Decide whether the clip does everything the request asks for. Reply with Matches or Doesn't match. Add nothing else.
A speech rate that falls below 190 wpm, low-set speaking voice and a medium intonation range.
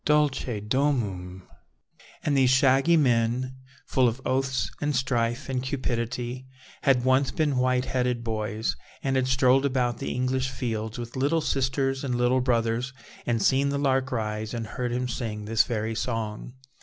Doesn't match